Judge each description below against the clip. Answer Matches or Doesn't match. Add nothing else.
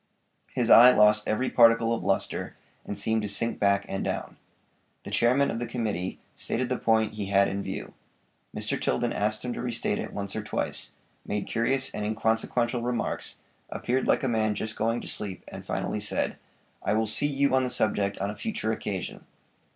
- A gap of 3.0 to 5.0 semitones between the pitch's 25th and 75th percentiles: Doesn't match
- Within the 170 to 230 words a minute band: Matches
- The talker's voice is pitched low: Matches